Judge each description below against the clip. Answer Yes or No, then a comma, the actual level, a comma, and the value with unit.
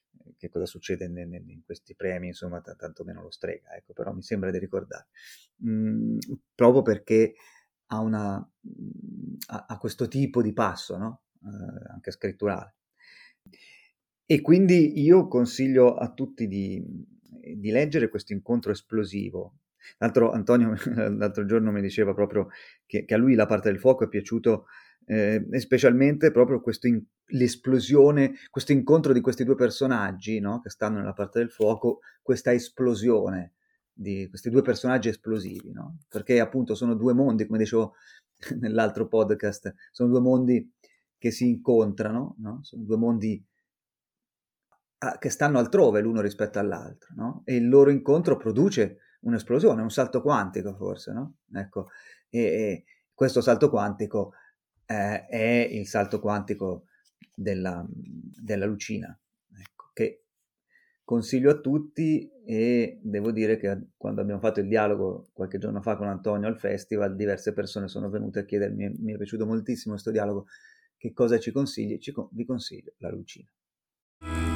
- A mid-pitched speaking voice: No, low, 115 Hz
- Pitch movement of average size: Yes, average, 3.9 semitones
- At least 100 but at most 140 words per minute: No, average, 150 wpm